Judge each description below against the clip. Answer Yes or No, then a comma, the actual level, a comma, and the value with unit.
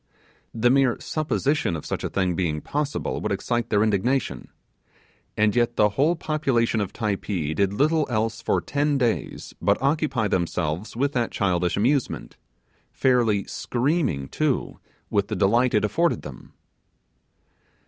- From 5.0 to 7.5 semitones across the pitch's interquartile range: Yes, wide, 5.6 semitones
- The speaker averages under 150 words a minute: Yes, average, 140 wpm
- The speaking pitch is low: Yes, low, 115 Hz